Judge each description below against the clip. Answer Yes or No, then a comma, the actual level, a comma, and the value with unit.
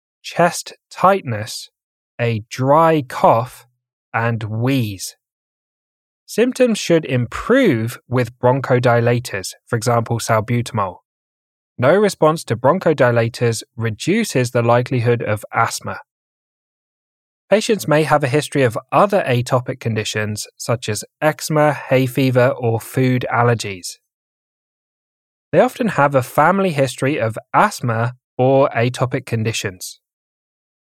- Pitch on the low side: Yes, low, 125 Hz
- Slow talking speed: Yes, slow, 100 wpm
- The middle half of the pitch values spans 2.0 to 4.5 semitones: Yes, average, 3.6 semitones